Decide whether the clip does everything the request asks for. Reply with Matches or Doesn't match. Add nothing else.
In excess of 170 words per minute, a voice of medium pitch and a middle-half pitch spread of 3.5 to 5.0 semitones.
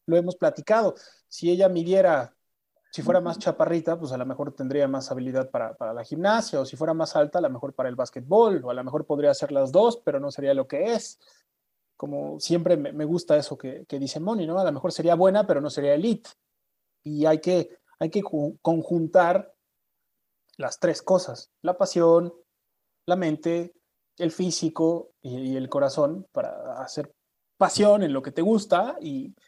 Matches